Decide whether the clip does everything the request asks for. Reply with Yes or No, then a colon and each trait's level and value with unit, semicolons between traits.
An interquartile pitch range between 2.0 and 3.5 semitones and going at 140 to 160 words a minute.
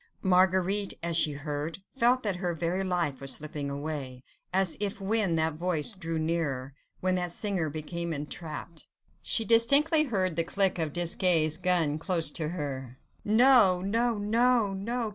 No: average, 4.4 semitones; average, 155 wpm